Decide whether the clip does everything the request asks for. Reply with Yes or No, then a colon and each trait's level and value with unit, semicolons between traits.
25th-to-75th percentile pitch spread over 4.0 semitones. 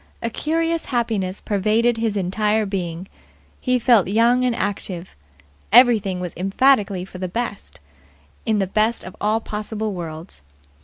No: average, 3.7 semitones